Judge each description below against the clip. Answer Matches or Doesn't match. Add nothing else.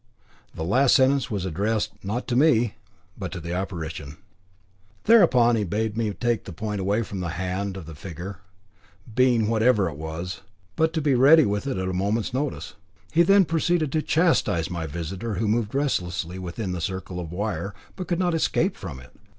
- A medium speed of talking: Matches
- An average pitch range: Doesn't match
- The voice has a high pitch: Doesn't match